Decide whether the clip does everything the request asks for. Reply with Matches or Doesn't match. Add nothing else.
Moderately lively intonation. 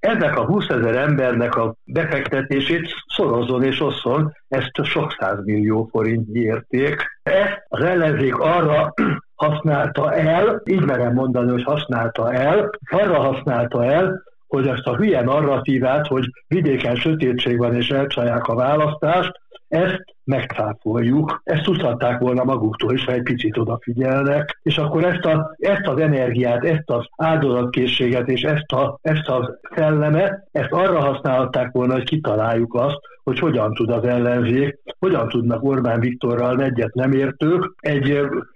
Matches